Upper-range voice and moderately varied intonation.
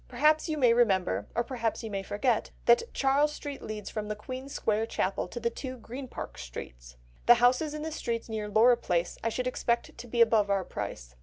Yes: high, 235 Hz; average, 3.5 semitones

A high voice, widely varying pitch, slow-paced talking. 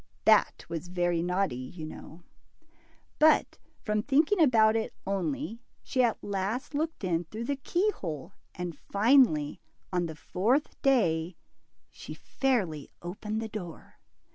Yes: high, 200 Hz; wide, 6.9 semitones; slow, 130 wpm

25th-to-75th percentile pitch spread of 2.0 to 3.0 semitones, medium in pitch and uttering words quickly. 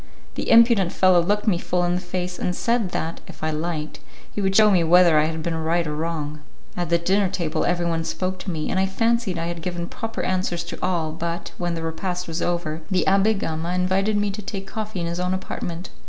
Yes: narrow, 2.4 semitones; medium, 175 Hz; fast, 230 wpm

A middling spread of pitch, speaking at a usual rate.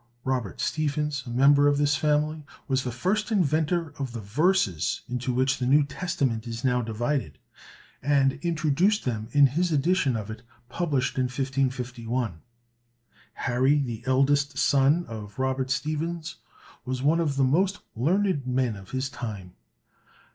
Yes: average, 3.4 semitones; average, 145 wpm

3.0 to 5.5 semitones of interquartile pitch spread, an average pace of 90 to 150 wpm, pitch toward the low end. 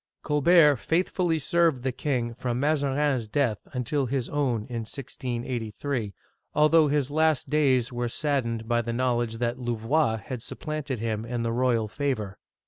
Yes: average, 4.0 semitones; average, 145 wpm; low, 125 Hz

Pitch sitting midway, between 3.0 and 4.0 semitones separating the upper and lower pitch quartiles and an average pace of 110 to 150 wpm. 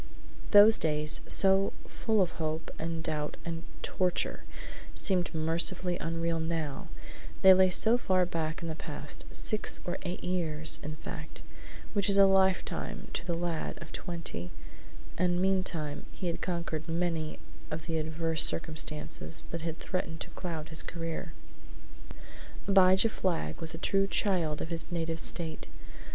No: medium, 165 Hz; narrow, 2.5 semitones; average, 145 wpm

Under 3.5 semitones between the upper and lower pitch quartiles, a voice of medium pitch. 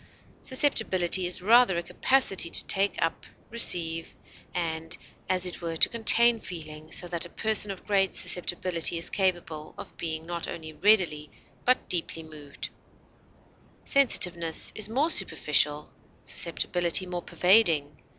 No: average, 3.8 semitones; medium, 175 Hz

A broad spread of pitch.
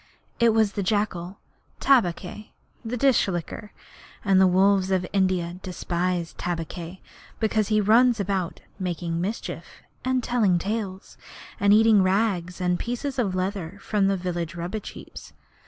No: average, 3.2 semitones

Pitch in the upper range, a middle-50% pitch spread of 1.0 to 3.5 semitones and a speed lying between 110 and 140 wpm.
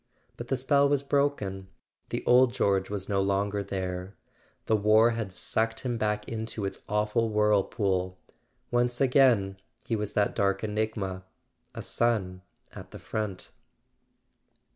No: low, 105 Hz; average, 3.2 semitones; slow, 135 wpm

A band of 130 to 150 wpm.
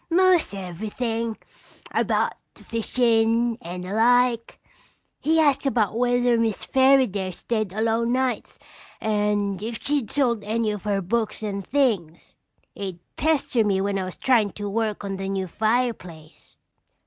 Yes: average, 140 wpm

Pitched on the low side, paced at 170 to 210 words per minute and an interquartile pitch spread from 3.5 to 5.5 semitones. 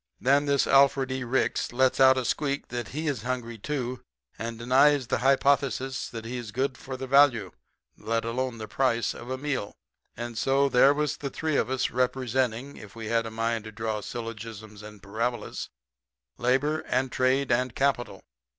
No: low, 125 Hz; average, 180 wpm; average, 2.7 semitones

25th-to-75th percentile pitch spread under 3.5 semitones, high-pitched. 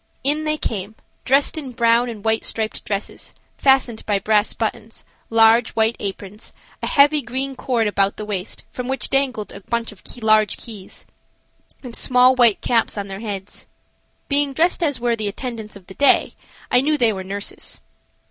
No: average, 3.8 semitones; high, 230 Hz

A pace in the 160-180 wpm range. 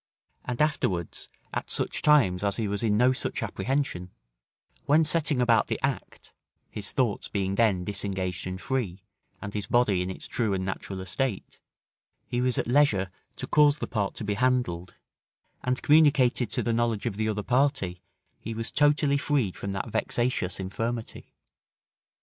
Yes: average, 165 wpm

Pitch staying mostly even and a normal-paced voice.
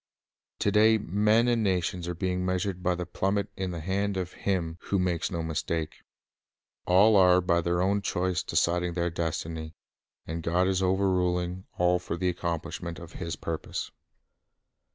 Yes: narrow, 1.9 semitones; average, 160 wpm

